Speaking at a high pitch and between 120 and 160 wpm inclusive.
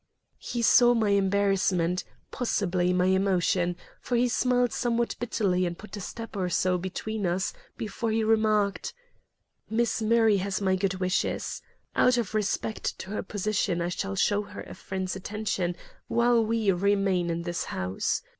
Yes: high, 200 Hz; average, 155 wpm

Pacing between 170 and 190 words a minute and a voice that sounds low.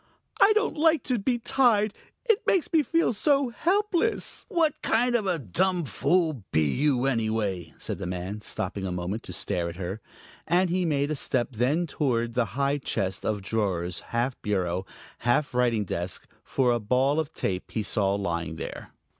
Yes: average, 180 wpm; low, 125 Hz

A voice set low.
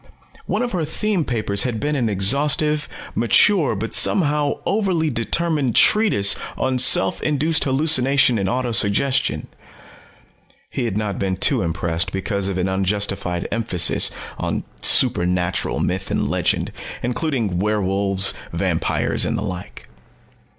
Yes: low, 115 Hz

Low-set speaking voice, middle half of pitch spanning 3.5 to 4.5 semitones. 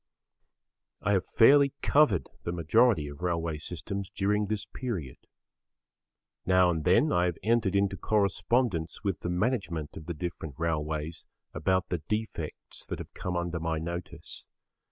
Yes: very low, 90 Hz; average, 4.1 semitones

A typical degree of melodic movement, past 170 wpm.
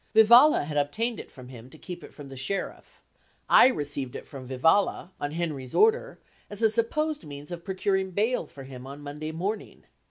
No: wide, 7.4 semitones; average, 190 wpm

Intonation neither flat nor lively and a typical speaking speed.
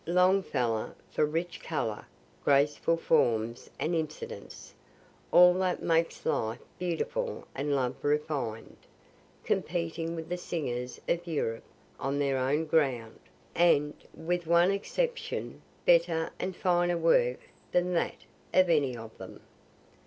No: average, 4.5 semitones; slow, 120 wpm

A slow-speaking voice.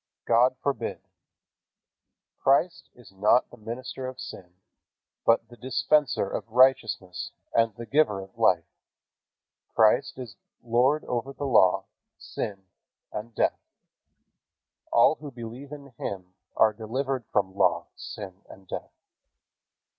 Yes: slow, 115 wpm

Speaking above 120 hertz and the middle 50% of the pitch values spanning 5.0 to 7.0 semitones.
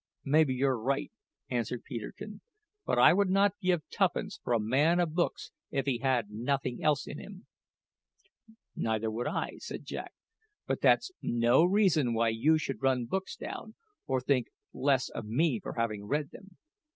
Yes: low, 135 Hz; average, 5.3 semitones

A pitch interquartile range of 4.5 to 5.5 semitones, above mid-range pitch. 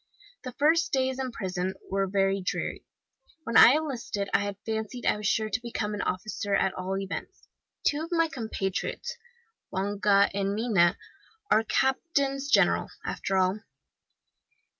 Yes: average, 5.1 semitones; high, 210 Hz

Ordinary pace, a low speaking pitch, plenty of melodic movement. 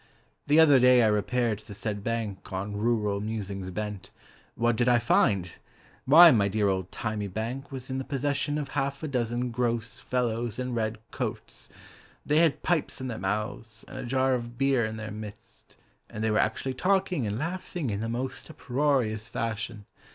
No: average, 185 wpm; low, 120 Hz; average, 3.7 semitones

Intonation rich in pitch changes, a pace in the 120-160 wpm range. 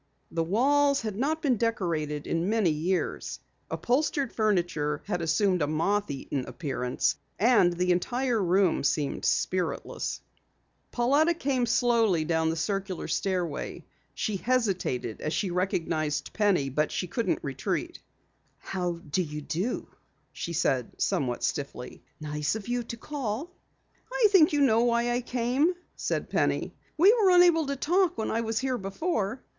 Yes: wide, 7.3 semitones; average, 145 wpm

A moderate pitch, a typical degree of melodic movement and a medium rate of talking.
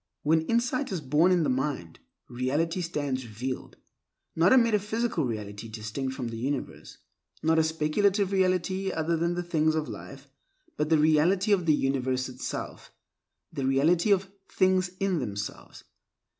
No: medium, 160 Hz; wide, 5.8 semitones; average, 150 wpm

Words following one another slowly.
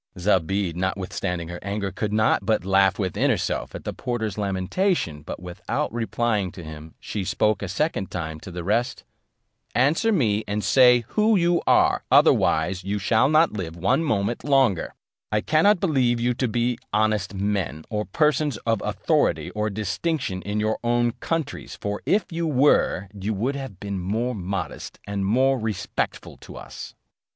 No: average, 165 wpm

